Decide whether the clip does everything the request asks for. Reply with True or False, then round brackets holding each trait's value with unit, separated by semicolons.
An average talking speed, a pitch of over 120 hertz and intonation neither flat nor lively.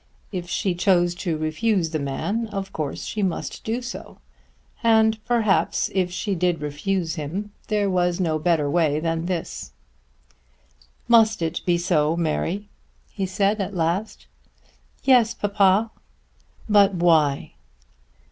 False (130 wpm; 185 Hz; 4.1 semitones)